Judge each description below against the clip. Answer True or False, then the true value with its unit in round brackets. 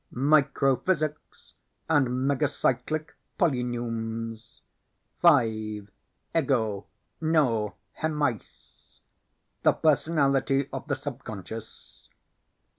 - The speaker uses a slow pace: True (60 wpm)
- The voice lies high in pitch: False (130 Hz)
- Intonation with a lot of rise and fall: False (4.7 semitones)